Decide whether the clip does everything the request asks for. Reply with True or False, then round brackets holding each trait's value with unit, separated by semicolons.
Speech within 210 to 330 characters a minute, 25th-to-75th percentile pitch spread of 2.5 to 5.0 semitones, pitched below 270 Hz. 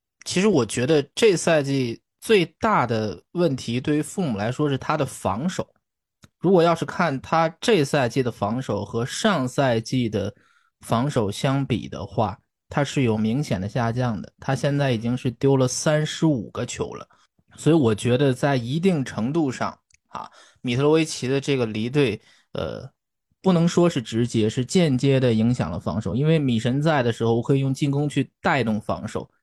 True (260 characters per minute; 4.4 semitones; 135 Hz)